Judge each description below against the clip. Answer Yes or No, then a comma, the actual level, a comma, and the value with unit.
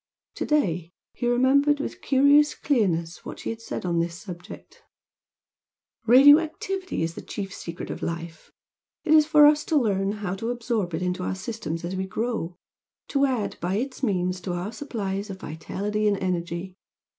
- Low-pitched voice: No, high, 205 Hz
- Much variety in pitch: Yes, wide, 7.0 semitones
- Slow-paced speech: No, average, 175 wpm